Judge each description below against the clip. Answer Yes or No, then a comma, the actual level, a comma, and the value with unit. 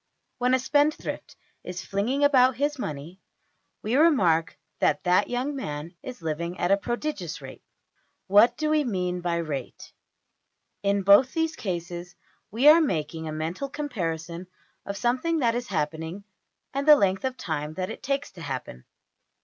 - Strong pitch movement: Yes, wide, 7.6 semitones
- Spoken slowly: No, average, 160 wpm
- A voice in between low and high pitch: No, high, 200 Hz